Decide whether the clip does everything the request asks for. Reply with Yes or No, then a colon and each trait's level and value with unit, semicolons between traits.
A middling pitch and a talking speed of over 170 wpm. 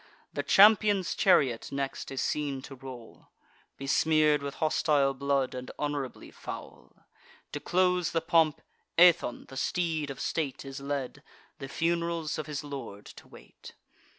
No: medium, 145 Hz; average, 140 wpm